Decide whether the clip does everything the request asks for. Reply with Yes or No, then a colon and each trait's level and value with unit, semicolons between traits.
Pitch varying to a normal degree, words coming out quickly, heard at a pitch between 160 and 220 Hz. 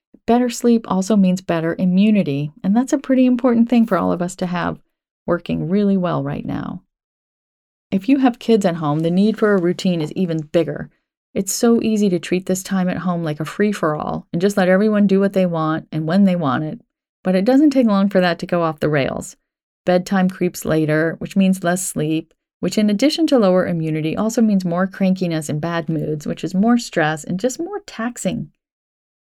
Yes: average, 4.4 semitones; fast, 215 wpm; high, 190 Hz